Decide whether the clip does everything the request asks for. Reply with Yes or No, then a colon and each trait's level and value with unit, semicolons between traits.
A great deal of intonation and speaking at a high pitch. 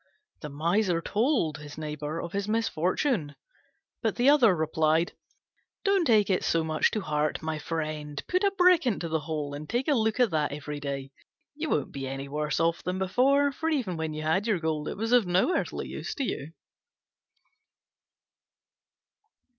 No: wide, 7.3 semitones; medium, 170 Hz